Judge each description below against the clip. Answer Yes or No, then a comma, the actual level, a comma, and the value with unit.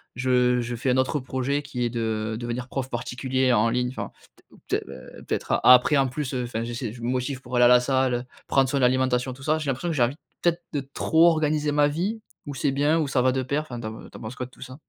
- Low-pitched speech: Yes, low, 130 Hz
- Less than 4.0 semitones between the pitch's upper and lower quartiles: Yes, narrow, 2.5 semitones